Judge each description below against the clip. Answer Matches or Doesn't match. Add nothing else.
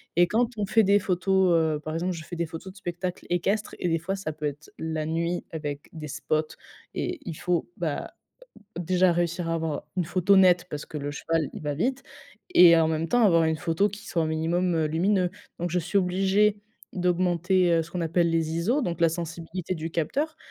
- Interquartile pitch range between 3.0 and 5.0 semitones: Doesn't match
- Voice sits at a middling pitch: Matches